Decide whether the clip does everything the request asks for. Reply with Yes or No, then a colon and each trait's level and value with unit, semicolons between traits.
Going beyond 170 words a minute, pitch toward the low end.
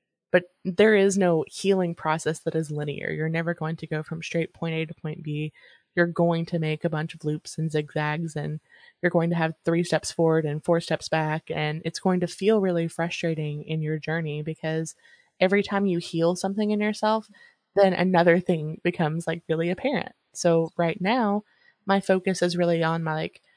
No: average, 200 wpm; medium, 165 Hz